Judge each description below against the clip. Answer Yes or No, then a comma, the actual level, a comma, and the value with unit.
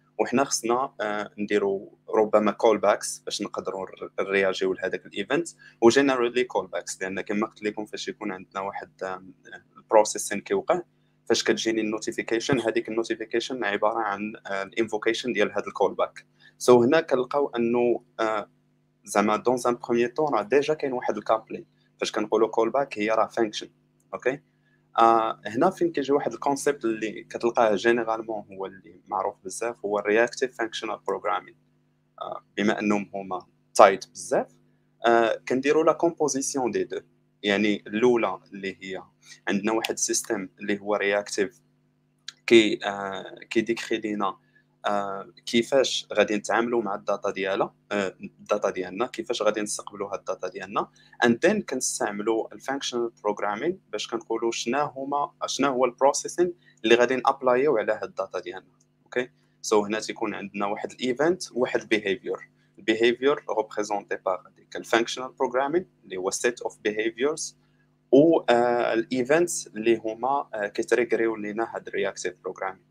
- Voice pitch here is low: Yes, low, 115 Hz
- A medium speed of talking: No, fast, 145 wpm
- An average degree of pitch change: Yes, average, 3.3 semitones